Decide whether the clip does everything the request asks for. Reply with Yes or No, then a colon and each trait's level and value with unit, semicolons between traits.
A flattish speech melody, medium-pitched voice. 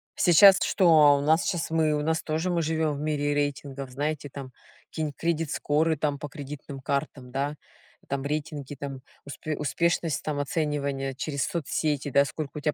Yes: narrow, 2.0 semitones; medium, 150 Hz